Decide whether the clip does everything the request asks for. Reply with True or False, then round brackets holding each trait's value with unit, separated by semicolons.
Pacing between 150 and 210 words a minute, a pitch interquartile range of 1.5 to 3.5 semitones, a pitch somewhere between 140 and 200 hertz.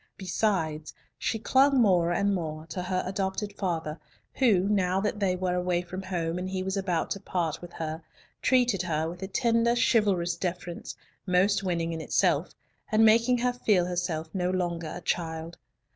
True (175 wpm; 2.8 semitones; 185 Hz)